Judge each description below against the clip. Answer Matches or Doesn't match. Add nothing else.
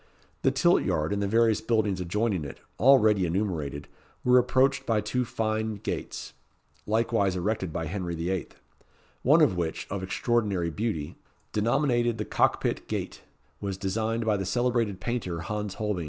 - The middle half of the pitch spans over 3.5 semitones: Matches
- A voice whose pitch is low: Matches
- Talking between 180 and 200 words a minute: Doesn't match